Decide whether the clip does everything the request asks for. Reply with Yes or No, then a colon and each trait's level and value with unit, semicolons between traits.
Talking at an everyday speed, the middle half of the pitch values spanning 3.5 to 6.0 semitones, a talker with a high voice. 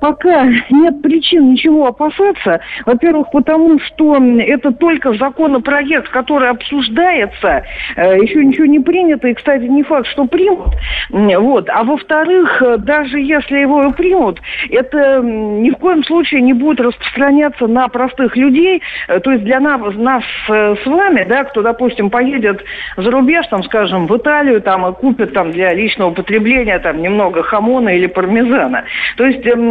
Yes: average, 145 wpm; average, 4.5 semitones; very high, 265 Hz